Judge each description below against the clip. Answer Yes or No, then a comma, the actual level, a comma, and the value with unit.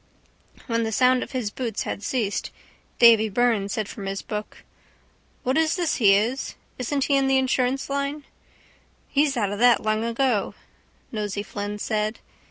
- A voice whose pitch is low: No, high, 235 Hz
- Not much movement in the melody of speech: No, average, 4.0 semitones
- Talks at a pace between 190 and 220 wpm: No, average, 165 wpm